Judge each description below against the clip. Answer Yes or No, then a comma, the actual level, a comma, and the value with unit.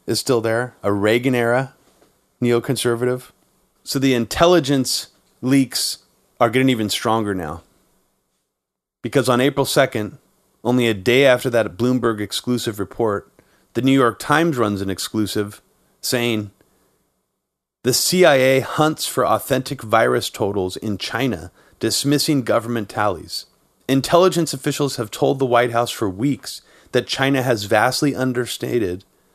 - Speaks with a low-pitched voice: Yes, low, 125 Hz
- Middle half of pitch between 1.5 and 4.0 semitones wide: Yes, average, 3.3 semitones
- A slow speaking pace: Yes, slow, 125 wpm